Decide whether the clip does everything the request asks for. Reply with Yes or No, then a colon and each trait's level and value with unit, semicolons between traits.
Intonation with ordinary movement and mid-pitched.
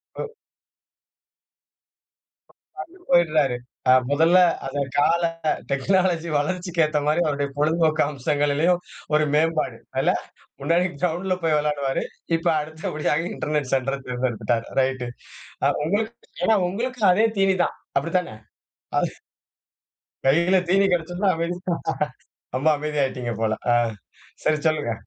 Yes: average, 3.8 semitones; medium, 155 Hz